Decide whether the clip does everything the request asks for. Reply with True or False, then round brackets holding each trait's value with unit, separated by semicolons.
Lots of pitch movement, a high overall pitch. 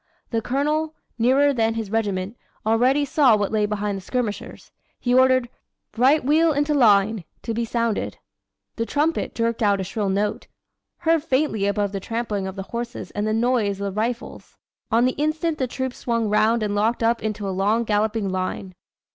False (3.8 semitones; 225 Hz)